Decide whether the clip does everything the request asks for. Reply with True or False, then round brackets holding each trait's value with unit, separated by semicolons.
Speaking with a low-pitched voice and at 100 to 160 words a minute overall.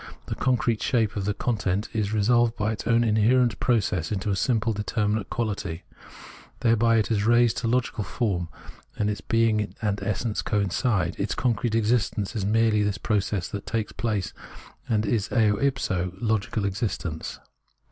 True (110 Hz; 155 wpm)